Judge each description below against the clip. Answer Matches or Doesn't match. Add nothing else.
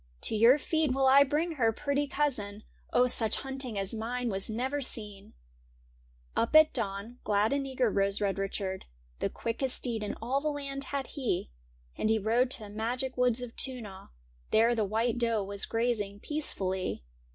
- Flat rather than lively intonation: Doesn't match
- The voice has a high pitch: Matches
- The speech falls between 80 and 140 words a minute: Doesn't match